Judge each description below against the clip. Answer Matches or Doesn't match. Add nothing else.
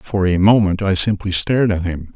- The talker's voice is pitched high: Doesn't match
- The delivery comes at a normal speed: Doesn't match